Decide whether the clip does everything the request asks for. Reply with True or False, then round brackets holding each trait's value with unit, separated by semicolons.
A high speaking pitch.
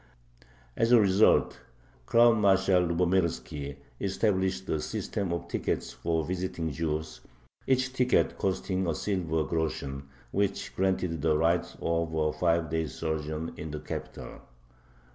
False (85 Hz)